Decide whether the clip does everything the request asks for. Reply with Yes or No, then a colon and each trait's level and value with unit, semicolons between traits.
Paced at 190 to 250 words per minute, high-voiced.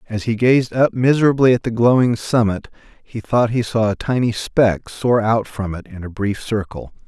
No: fast, 205 wpm; low, 115 Hz